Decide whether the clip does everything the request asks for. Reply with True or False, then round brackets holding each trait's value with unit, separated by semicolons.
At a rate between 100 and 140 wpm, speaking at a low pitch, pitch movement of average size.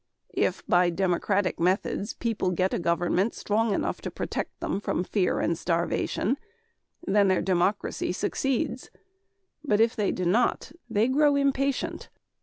False (135 wpm; 200 Hz; 4.4 semitones)